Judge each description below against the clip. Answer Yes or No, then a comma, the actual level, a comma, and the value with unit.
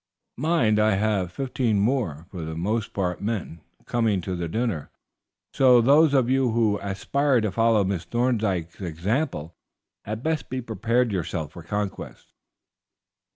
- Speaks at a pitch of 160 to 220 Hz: No, low, 110 Hz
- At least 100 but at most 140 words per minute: Yes, slow, 135 wpm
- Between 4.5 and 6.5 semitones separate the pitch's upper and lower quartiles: Yes, average, 5.2 semitones